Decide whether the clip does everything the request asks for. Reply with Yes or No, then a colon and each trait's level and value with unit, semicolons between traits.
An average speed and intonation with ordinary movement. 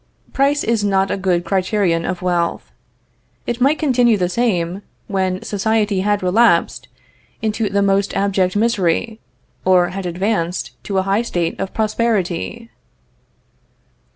No: slow, 130 wpm; average, 3.3 semitones